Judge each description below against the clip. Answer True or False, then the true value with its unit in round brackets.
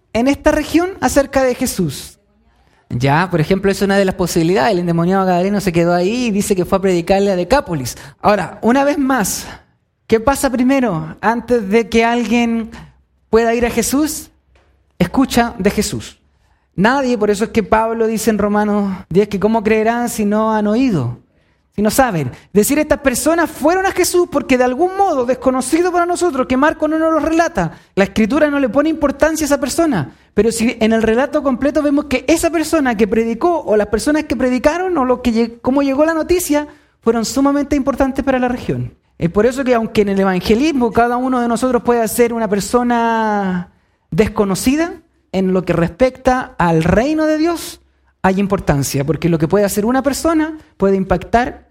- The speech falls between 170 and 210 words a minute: True (185 wpm)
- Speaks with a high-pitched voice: True (235 Hz)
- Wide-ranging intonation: True (5.9 semitones)